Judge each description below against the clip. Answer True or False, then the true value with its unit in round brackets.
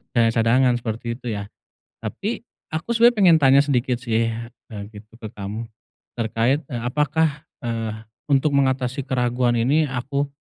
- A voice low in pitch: True (125 Hz)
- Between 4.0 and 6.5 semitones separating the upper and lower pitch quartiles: False (3.4 semitones)